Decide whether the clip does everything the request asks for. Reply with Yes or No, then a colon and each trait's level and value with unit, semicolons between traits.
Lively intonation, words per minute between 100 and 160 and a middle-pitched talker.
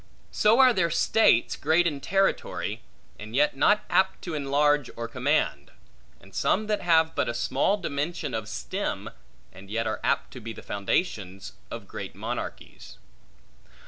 Yes: wide, 7.4 semitones; average, 150 wpm; medium, 145 Hz